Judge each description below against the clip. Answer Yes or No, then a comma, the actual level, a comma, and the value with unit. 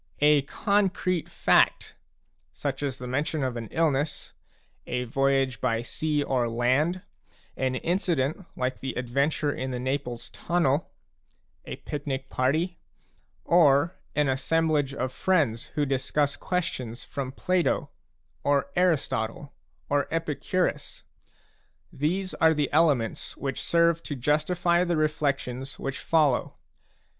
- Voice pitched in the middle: Yes, medium, 145 Hz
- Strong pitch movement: No, average, 3.8 semitones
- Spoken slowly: Yes, slow, 120 wpm